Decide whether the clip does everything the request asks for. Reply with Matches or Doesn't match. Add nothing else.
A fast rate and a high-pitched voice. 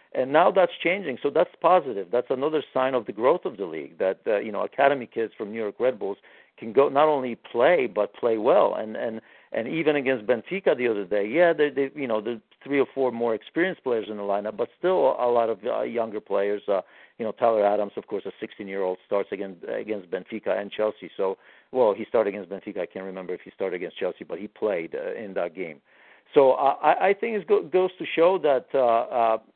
Doesn't match